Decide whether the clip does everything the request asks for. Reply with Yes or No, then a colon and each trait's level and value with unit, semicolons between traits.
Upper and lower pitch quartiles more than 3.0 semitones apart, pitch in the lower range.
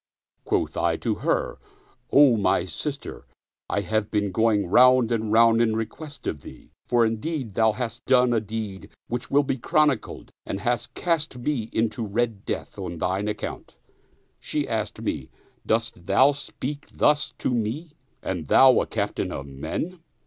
Yes: average, 4.5 semitones; low, 115 Hz